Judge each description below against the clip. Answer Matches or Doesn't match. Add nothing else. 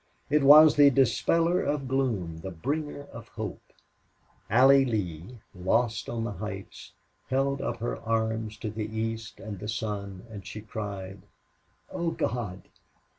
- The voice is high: Doesn't match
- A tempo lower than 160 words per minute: Matches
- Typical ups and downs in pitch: Matches